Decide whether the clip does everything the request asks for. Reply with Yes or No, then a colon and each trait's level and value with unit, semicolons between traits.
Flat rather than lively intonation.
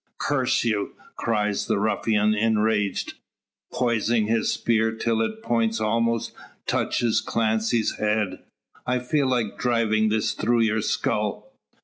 Yes: narrow, 1.4 semitones